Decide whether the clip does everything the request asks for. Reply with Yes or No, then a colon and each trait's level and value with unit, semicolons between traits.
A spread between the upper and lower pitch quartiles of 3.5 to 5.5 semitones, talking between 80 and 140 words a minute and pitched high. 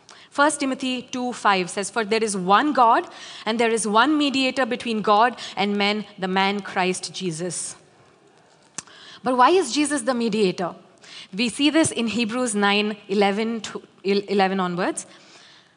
Yes: average, 4.2 semitones; slow, 135 wpm; high, 220 Hz